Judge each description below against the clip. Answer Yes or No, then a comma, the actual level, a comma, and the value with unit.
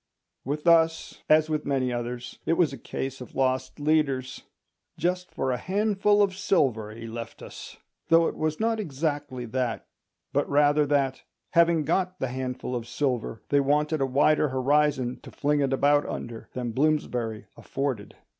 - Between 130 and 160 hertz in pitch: Yes, medium, 140 Hz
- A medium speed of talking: Yes, average, 165 wpm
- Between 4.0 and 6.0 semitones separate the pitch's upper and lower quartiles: No, average, 3.6 semitones